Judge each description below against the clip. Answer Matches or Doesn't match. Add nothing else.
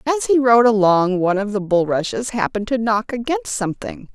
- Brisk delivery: Doesn't match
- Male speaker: Doesn't match